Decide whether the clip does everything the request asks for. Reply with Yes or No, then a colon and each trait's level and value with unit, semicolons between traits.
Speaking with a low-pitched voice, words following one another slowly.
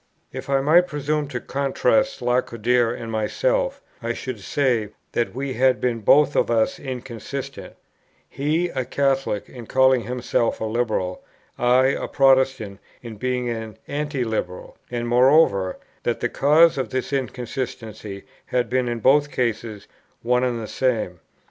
No: low, 125 Hz; average, 150 wpm